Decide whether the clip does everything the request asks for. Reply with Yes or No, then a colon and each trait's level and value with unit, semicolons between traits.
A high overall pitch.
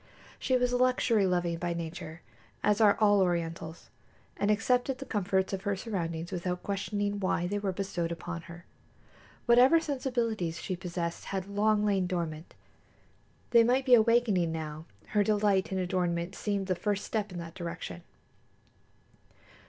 Yes: high, 195 Hz